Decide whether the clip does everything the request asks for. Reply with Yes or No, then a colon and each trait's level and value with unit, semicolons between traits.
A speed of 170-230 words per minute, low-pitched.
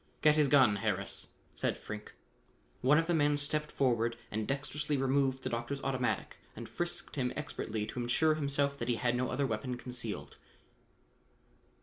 No: average, 160 wpm; low, 130 Hz